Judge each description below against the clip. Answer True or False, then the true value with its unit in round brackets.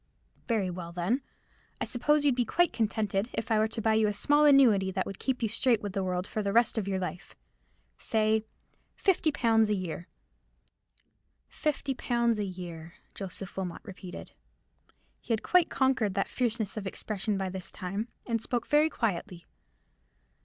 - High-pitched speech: True (215 Hz)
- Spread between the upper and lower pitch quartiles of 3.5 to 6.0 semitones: True (4.0 semitones)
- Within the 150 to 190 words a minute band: True (175 wpm)